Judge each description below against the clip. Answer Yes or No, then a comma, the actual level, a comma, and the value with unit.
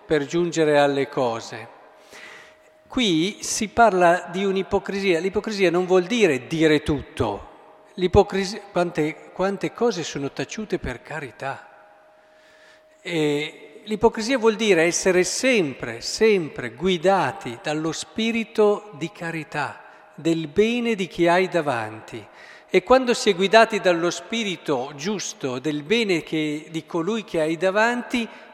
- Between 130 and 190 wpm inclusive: No, average, 120 wpm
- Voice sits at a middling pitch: Yes, medium, 180 Hz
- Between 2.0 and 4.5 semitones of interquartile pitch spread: No, average, 5.1 semitones